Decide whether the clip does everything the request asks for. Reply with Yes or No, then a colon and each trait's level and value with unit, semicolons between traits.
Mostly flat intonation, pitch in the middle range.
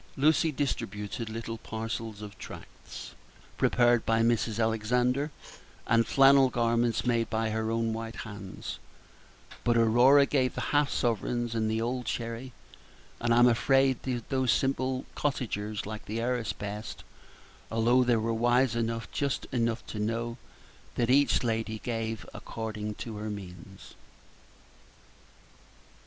No: narrow, 2.0 semitones; low, 115 Hz